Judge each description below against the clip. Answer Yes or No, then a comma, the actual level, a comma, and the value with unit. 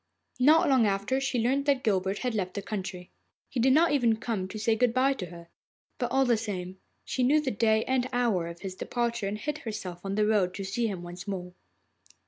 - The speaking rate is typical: No, fast, 225 wpm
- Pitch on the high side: Yes, high, 220 Hz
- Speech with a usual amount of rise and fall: Yes, average, 5.0 semitones